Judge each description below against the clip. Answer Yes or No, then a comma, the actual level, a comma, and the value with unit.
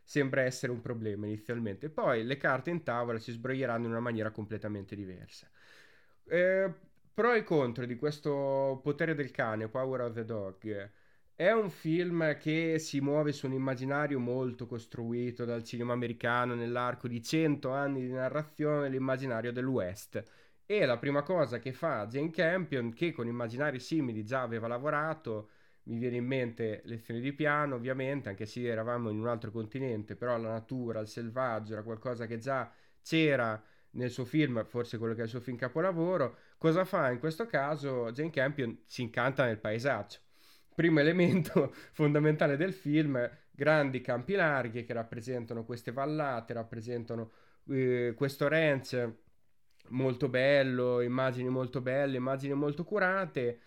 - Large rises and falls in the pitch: No, average, 3.7 semitones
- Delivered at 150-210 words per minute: Yes, average, 155 wpm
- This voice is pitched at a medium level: No, low, 130 Hz